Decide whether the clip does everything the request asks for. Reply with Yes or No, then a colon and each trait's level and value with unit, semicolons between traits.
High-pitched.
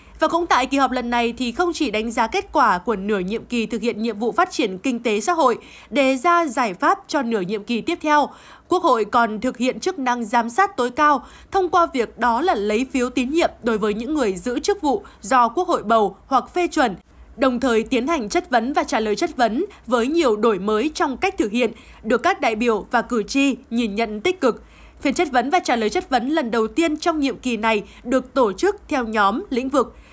Yes: very high, 255 Hz